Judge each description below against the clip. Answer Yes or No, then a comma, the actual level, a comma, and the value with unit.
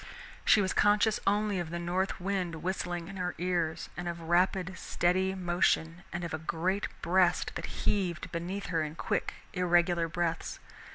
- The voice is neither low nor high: Yes, medium, 175 Hz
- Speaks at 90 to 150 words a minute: No, average, 165 wpm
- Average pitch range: No, narrow, 1.8 semitones